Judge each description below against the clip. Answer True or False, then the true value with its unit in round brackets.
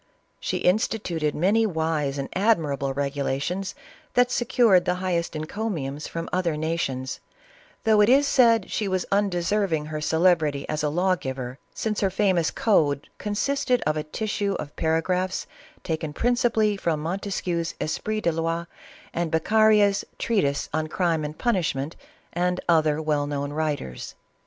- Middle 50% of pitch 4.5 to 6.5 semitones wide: True (5.0 semitones)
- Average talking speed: True (150 wpm)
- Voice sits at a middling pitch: True (170 Hz)